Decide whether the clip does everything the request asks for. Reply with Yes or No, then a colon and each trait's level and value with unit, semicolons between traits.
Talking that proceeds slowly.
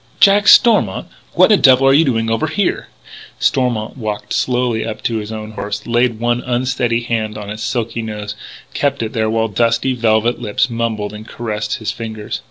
No: average, 180 wpm